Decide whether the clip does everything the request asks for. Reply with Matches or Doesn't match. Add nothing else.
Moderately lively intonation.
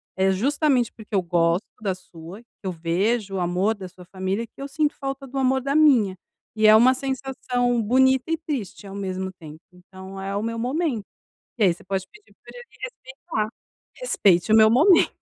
Doesn't match